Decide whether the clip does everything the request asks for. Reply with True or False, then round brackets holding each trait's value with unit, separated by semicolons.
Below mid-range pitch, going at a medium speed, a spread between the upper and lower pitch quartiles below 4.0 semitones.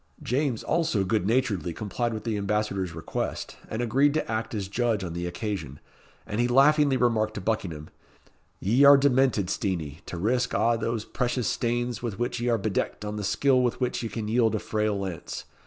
True (110 Hz; 190 wpm; 3.6 semitones)